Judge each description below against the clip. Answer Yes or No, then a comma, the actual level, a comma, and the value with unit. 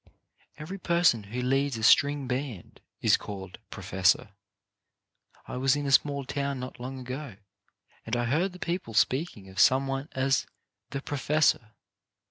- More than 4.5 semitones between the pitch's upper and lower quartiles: No, average, 3.4 semitones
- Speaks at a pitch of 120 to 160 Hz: Yes, low, 135 Hz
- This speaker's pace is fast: No, average, 165 wpm